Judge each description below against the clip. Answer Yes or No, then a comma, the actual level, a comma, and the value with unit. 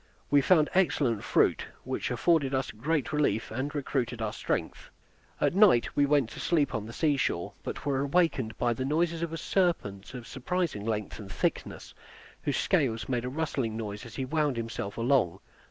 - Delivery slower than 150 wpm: No, average, 185 wpm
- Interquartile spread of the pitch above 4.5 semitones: Yes, average, 5.2 semitones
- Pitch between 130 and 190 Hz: Yes, low, 135 Hz